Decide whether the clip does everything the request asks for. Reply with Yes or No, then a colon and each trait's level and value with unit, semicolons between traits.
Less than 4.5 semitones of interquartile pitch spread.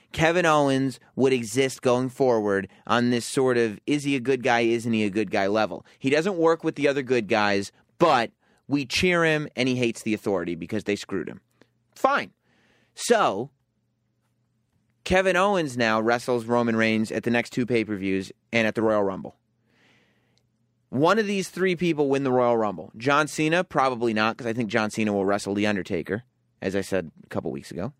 Yes: average, 4.0 semitones